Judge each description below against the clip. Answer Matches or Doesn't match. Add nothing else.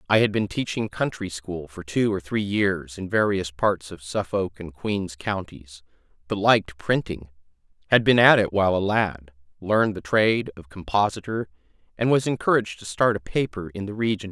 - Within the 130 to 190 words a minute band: Doesn't match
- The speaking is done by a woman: Doesn't match